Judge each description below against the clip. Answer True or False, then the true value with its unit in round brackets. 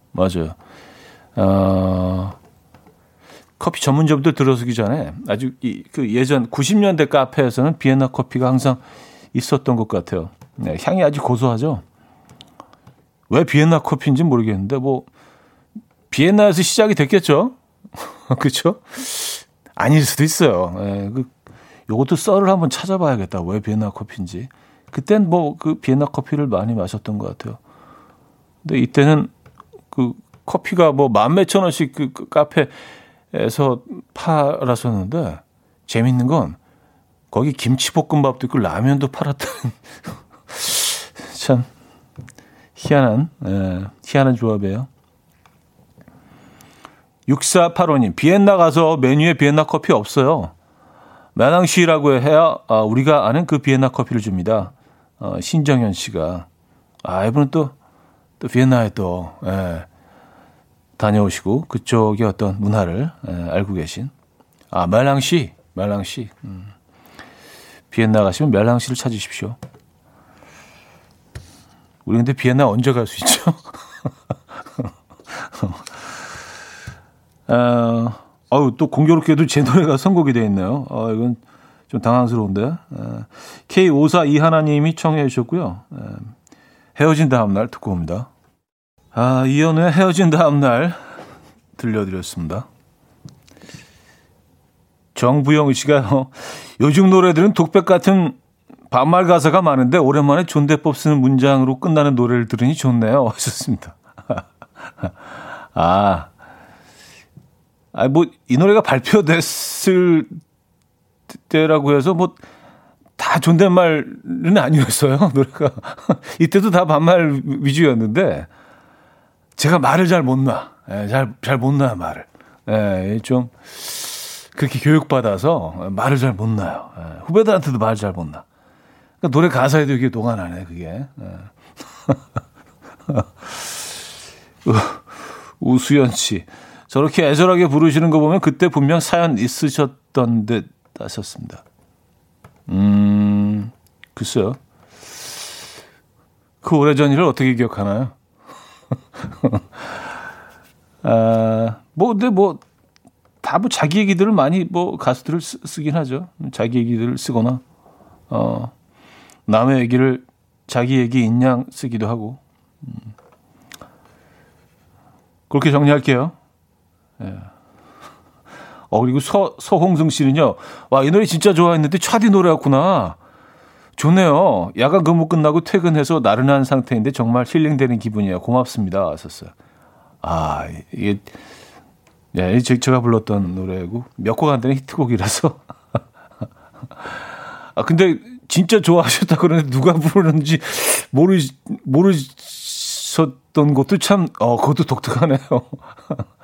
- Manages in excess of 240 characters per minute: False (235 characters per minute)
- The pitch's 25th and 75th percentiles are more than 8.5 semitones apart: False (5.9 semitones)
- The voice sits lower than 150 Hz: True (135 Hz)